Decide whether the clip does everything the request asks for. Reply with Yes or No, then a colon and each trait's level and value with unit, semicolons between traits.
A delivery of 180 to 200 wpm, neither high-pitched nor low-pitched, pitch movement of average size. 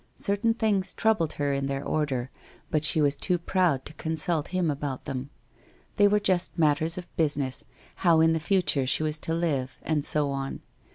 Yes: average, 185 wpm; medium, 155 Hz; average, 3.8 semitones